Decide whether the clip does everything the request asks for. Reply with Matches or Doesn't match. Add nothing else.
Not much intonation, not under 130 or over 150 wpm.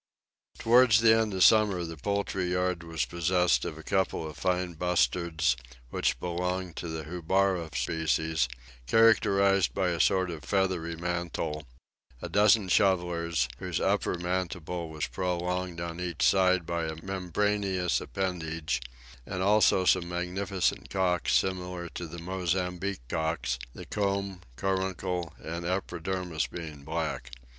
Matches